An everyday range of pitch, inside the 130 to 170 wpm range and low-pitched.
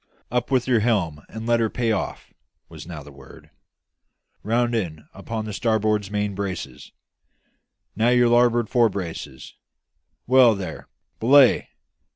Yes: average, 3.7 semitones; average, 140 wpm; low, 110 Hz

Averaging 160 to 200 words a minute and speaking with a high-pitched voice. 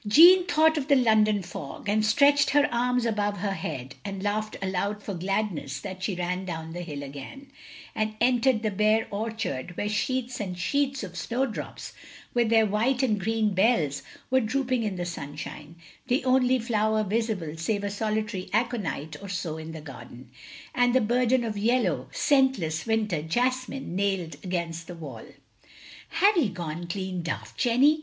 Yes: average, 170 wpm; high, 210 Hz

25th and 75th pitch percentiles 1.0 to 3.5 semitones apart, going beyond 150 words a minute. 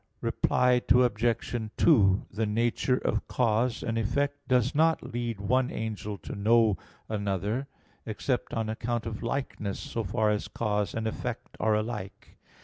No: average, 2.7 semitones; average, 140 wpm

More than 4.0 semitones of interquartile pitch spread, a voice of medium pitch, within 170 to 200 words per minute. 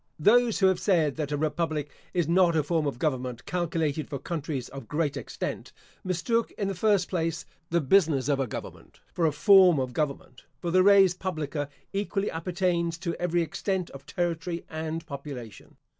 No: average, 3.7 semitones; medium, 165 Hz; average, 175 wpm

